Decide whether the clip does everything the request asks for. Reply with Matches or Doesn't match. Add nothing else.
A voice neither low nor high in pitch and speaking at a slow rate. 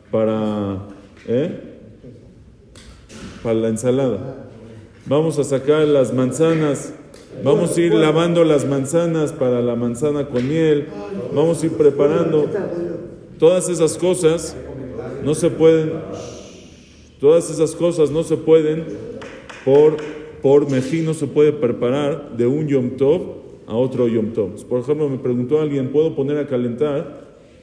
Matches